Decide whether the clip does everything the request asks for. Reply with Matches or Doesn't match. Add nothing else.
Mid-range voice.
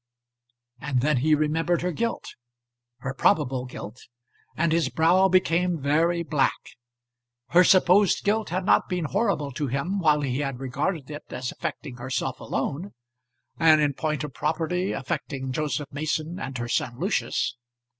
Matches